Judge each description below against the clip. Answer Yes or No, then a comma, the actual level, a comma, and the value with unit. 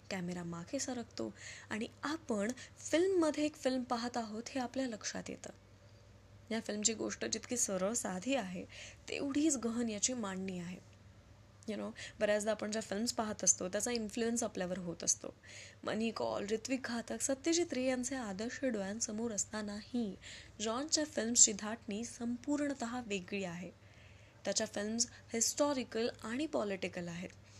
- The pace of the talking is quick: Yes, fast, 135 wpm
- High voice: Yes, high, 220 Hz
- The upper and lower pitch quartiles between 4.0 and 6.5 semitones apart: Yes, average, 5.2 semitones